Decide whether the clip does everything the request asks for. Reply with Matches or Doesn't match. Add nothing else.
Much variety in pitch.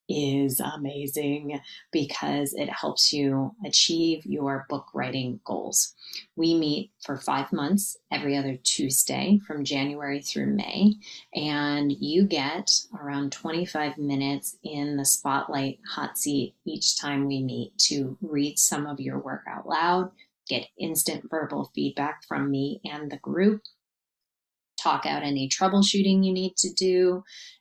Doesn't match